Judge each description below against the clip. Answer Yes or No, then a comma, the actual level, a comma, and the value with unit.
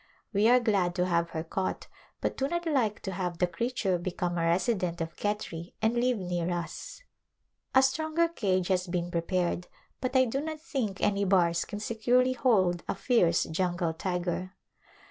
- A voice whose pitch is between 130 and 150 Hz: No, high, 190 Hz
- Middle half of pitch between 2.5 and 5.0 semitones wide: No, wide, 5.6 semitones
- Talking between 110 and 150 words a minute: No, average, 175 wpm